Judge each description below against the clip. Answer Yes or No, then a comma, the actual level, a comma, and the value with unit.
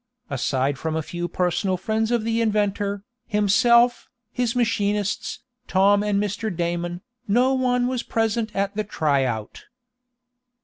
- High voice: Yes, high, 205 Hz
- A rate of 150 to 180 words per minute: No, slow, 135 wpm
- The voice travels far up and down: No, average, 4.5 semitones